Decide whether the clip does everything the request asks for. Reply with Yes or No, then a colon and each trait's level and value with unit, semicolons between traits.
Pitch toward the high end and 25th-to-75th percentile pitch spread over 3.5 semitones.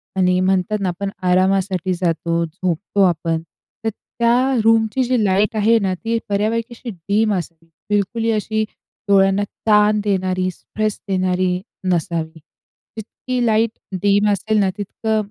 No: high, 200 Hz; average, 3.1 semitones